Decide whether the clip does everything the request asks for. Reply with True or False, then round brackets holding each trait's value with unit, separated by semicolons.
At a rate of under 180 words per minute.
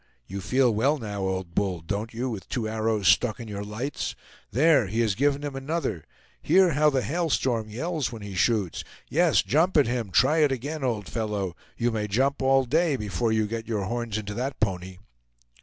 False (200 wpm)